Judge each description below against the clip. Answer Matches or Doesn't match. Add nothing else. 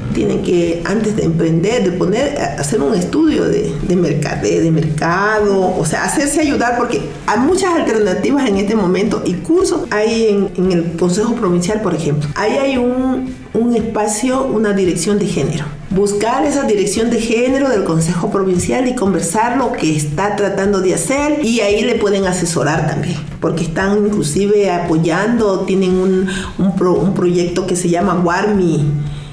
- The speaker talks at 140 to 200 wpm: Matches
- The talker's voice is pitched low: Doesn't match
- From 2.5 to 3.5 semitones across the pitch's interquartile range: Doesn't match